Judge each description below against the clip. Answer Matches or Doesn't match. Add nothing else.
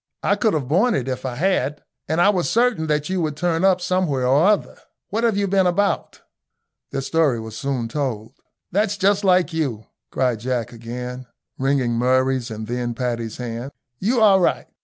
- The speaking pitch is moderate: Matches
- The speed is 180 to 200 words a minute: Matches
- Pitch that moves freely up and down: Matches